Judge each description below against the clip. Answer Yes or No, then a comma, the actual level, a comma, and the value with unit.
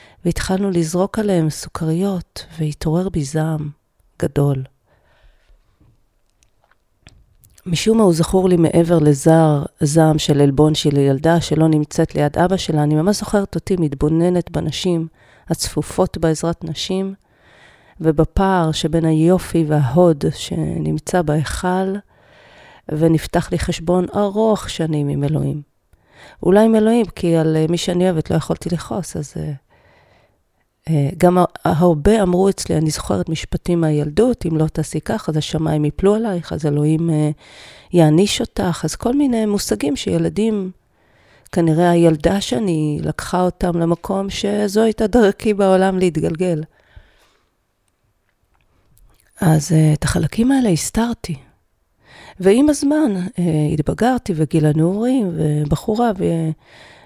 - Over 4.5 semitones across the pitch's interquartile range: No, average, 3.7 semitones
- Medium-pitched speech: Yes, medium, 165 Hz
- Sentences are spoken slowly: No, average, 120 wpm